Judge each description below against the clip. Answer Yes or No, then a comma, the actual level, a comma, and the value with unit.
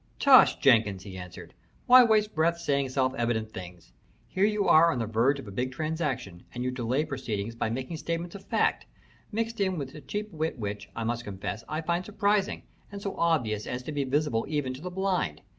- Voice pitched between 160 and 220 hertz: No, medium, 140 Hz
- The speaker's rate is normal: No, fast, 210 wpm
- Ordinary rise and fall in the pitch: No, wide, 7.0 semitones